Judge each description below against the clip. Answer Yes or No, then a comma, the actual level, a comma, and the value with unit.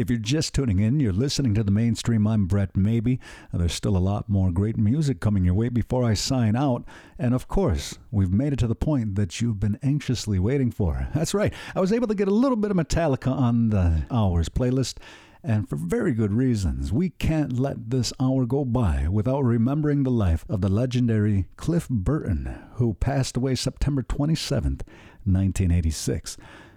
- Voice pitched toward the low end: Yes, low, 115 Hz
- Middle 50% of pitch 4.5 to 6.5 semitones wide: Yes, average, 4.9 semitones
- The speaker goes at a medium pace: Yes, average, 190 wpm